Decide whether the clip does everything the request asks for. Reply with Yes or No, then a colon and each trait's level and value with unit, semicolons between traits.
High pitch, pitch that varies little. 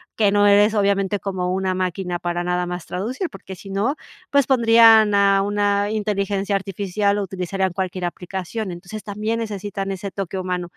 Yes: high, 195 Hz; narrow, 2.0 semitones